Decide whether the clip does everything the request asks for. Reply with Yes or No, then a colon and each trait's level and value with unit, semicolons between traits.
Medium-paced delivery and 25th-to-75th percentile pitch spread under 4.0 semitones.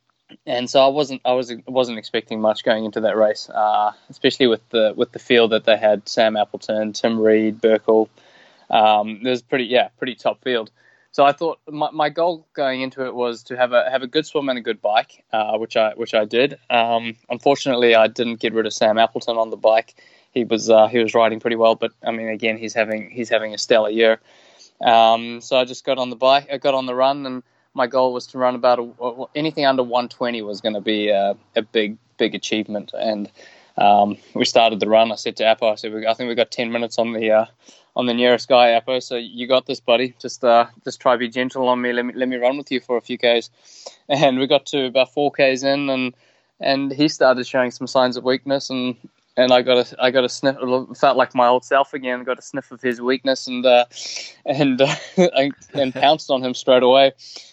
No: fast, 235 wpm; narrow, 2.6 semitones